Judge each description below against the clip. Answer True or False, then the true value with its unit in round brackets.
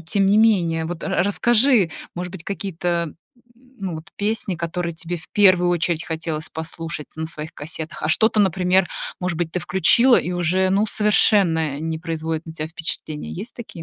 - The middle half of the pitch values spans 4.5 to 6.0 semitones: False (3.2 semitones)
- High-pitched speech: False (175 Hz)